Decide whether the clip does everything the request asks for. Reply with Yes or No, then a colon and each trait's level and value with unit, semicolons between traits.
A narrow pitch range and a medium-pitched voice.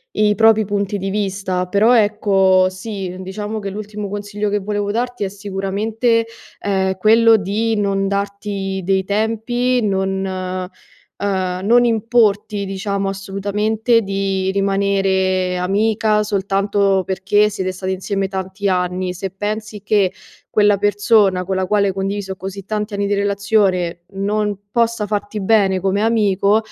No: narrow, 1.7 semitones; high, 200 Hz